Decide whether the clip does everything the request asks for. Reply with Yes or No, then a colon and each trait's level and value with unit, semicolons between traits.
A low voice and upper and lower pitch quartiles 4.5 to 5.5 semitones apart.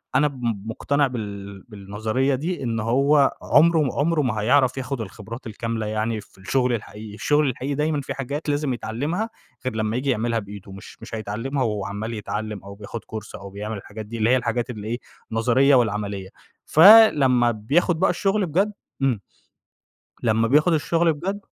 Yes: low, 120 Hz; average, 4.9 semitones